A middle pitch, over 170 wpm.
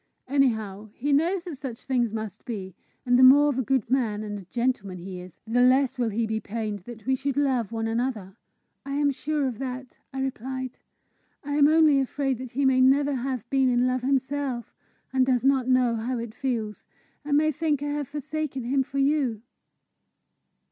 No: very high, 255 Hz; average, 195 wpm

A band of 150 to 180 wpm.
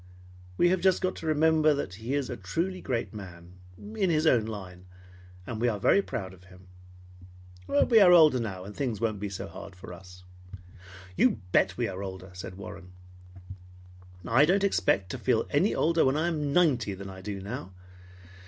No: average, 190 wpm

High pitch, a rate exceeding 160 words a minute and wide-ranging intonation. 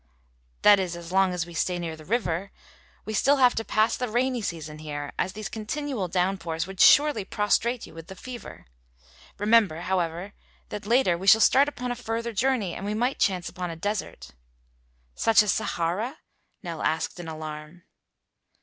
No: high, 195 Hz; average, 175 wpm; average, 5.0 semitones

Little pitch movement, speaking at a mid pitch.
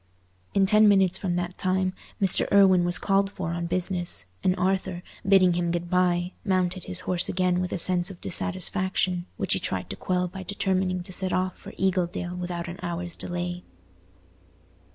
Yes: narrow, 1.2 semitones; medium, 180 Hz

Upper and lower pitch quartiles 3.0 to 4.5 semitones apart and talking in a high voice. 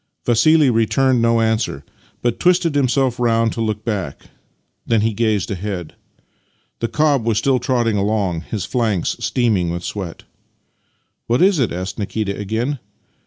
No: average, 3.5 semitones; low, 115 Hz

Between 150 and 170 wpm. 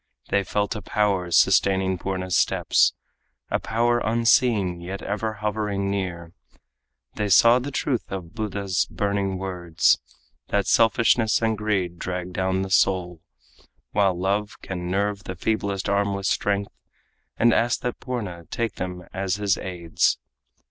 No: average, 140 wpm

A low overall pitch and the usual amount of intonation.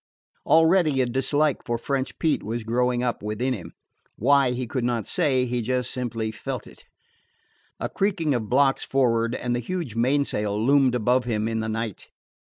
Yes: low, 125 Hz; average, 3.0 semitones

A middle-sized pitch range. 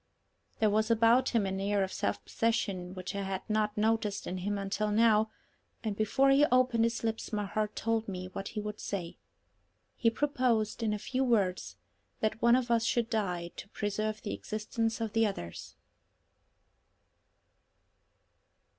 No: narrow, 2.2 semitones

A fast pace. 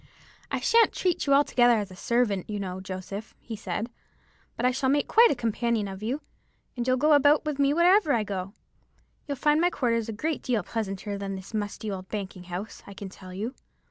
Yes: fast, 210 wpm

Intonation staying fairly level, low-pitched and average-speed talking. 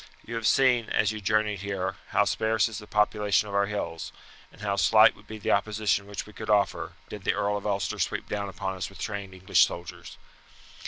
No: narrow, 1.4 semitones; low, 105 Hz; fast, 215 wpm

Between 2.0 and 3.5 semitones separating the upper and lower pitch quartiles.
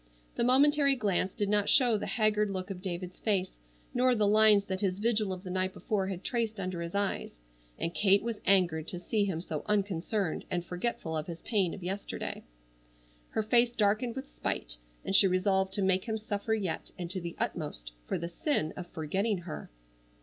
Yes: average, 3.1 semitones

